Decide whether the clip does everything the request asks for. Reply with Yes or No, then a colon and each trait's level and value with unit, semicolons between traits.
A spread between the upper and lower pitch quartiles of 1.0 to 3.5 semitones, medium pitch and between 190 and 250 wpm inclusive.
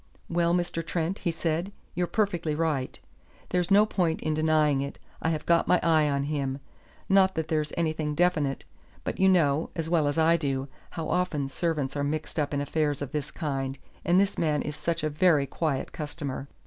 Yes: average, 2.8 semitones; medium, 155 Hz; average, 195 wpm